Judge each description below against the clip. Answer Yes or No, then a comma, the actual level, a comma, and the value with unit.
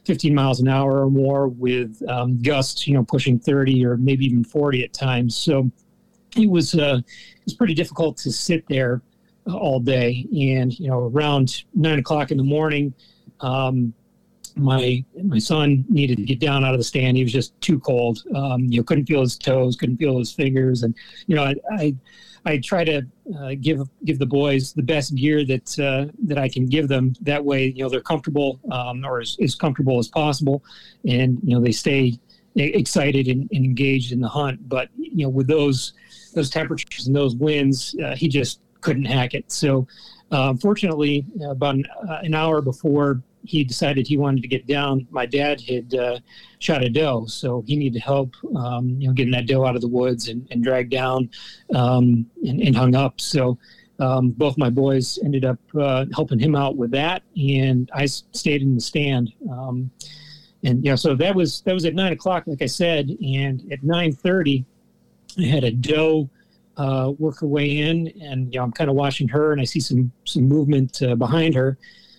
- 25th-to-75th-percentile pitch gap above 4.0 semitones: No, average, 3.2 semitones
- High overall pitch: No, low, 135 Hz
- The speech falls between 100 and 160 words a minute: No, fast, 205 wpm